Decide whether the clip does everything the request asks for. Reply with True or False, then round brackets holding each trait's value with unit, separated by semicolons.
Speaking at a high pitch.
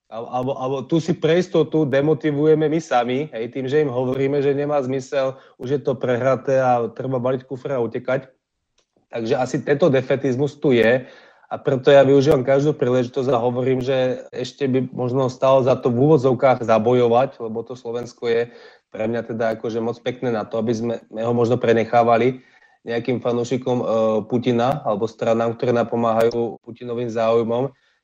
False (125 Hz)